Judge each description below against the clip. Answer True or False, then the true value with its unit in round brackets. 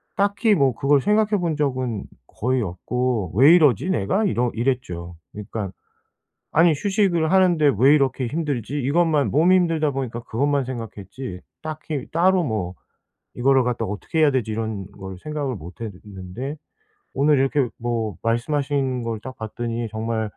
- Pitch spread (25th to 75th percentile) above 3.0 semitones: True (5.3 semitones)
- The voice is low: True (130 Hz)